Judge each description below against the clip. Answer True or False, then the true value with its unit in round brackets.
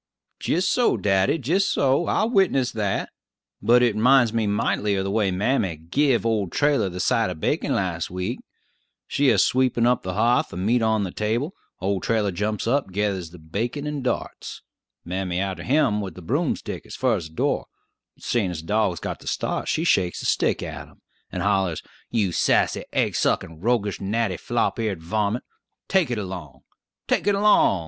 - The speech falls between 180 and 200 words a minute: True (190 wpm)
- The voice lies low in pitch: True (105 Hz)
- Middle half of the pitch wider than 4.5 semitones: True (5.0 semitones)